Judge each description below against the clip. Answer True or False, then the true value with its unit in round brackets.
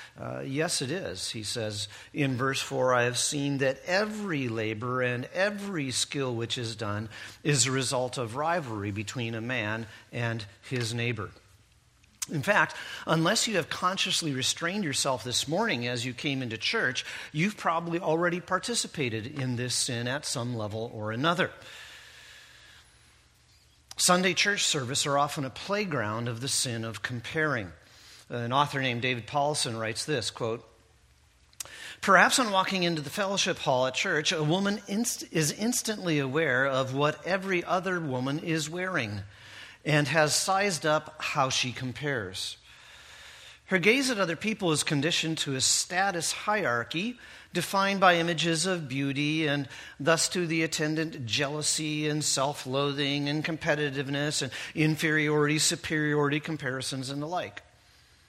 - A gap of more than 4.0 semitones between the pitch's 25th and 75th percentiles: True (5.5 semitones)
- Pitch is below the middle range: False (145 Hz)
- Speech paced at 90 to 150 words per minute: True (145 wpm)